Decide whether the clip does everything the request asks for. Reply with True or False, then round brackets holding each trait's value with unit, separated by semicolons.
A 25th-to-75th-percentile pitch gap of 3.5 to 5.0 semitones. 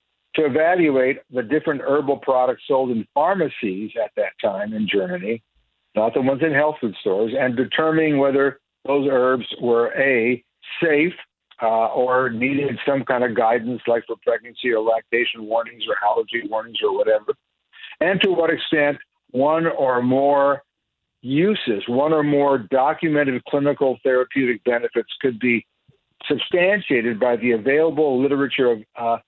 True (3.9 semitones)